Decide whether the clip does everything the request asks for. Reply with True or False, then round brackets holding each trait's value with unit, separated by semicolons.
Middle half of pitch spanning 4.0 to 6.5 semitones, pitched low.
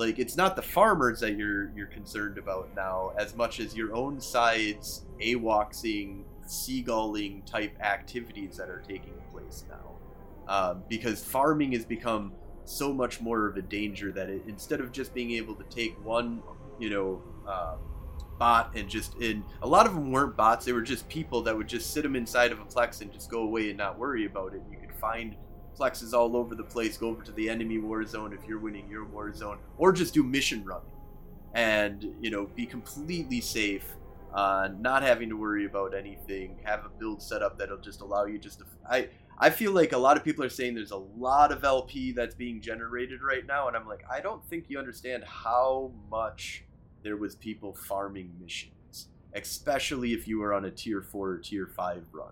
False (3.3 semitones; 110 Hz)